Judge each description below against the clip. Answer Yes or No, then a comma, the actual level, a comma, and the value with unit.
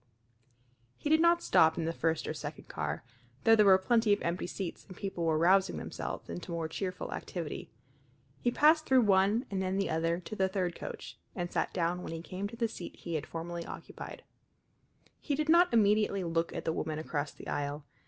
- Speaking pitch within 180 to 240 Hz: Yes, medium, 185 Hz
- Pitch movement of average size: Yes, average, 4.3 semitones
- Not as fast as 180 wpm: No, fast, 205 wpm